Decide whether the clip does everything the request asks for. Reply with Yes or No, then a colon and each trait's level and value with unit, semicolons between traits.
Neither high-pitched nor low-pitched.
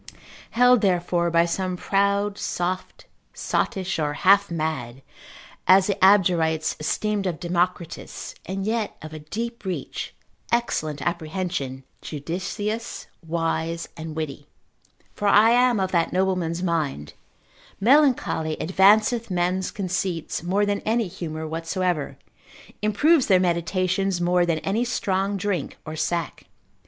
Yes: medium, 180 Hz